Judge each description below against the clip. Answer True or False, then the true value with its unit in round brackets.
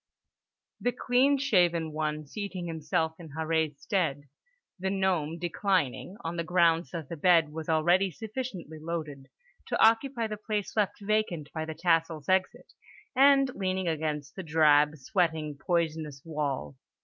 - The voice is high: False (165 Hz)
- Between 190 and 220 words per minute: False (140 wpm)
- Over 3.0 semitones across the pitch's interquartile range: True (3.8 semitones)